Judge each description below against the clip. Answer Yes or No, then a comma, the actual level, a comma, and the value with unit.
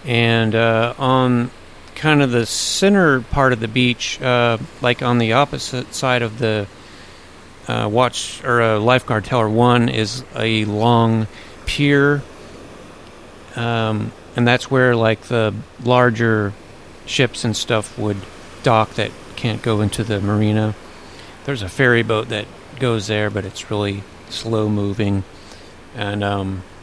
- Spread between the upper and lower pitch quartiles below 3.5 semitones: Yes, average, 3.1 semitones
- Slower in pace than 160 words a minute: Yes, average, 140 wpm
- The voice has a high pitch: No, low, 110 Hz